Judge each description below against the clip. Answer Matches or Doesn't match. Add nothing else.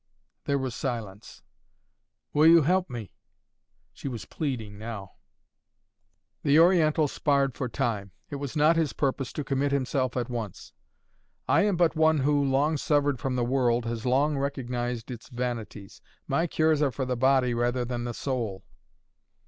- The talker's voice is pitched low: Matches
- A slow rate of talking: Doesn't match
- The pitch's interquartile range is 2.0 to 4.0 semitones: Matches